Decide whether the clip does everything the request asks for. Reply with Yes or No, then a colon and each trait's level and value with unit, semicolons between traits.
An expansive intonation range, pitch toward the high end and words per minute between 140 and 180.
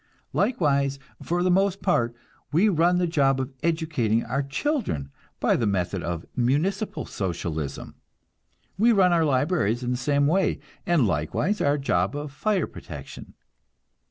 No: wide, 7.0 semitones; medium, 145 Hz; average, 145 wpm